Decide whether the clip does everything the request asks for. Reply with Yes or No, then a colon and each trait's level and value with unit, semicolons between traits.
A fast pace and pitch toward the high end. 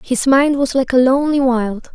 Yes: fast, 215 wpm; very high, 260 Hz